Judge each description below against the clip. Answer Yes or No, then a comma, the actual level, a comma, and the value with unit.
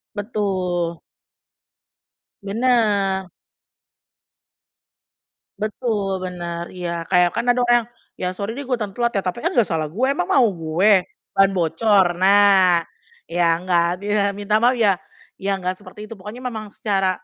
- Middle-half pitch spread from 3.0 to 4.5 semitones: Yes, average, 3.6 semitones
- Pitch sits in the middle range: No, high, 195 Hz